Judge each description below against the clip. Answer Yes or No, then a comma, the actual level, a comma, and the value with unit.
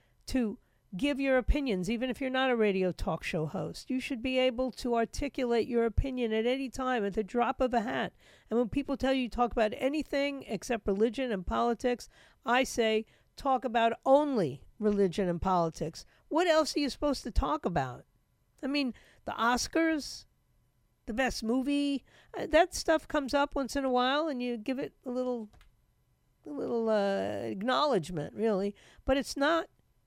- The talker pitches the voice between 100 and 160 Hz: No, very high, 250 Hz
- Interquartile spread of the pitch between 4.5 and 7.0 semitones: No, average, 3.6 semitones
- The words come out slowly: No, average, 175 wpm